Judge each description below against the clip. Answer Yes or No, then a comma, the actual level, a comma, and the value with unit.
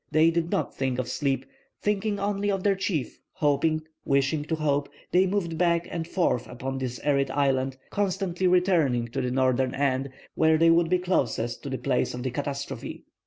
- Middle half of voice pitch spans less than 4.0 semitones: No, average, 5.0 semitones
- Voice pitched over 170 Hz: No, medium, 150 Hz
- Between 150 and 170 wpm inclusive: No, average, 185 wpm